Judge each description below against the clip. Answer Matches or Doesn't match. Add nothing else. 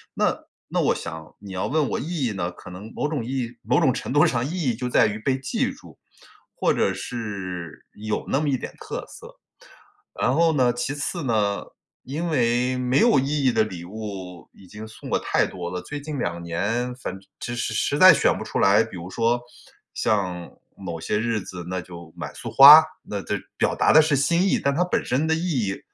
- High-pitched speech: Doesn't match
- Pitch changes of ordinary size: Doesn't match